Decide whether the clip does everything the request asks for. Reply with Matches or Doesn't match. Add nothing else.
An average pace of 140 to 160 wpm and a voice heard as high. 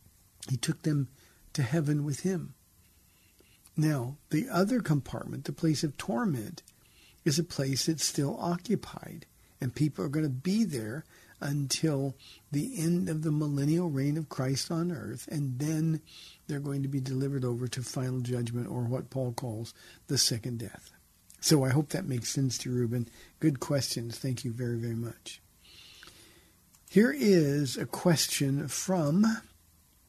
Doesn't match